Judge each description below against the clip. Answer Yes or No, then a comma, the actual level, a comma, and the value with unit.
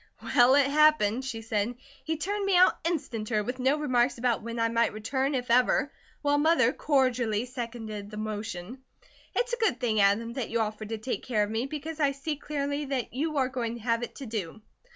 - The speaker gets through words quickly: Yes, fast, 210 wpm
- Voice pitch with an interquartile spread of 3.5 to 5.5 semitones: Yes, average, 4.2 semitones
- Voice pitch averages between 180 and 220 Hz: No, high, 245 Hz